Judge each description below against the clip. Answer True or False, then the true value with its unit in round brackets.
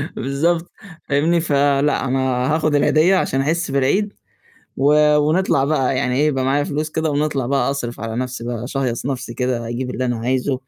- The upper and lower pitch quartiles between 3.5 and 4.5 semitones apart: False (3.0 semitones)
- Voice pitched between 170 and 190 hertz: False (140 Hz)